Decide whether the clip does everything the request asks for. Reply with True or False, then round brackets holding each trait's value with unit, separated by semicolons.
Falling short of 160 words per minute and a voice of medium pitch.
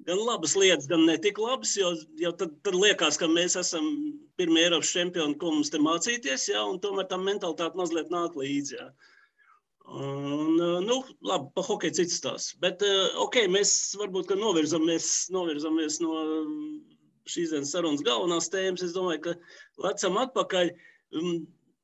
True (135 wpm; 175 Hz)